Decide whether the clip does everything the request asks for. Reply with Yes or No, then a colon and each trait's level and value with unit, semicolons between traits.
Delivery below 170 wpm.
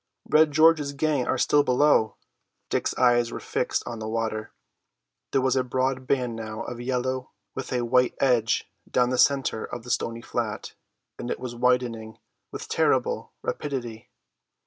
Yes: average, 160 wpm